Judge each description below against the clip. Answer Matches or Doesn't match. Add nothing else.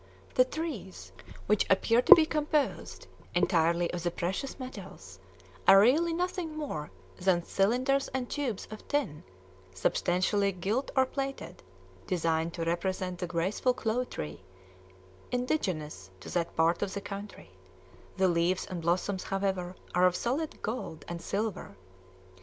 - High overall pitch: Matches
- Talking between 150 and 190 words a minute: Doesn't match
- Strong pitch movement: Matches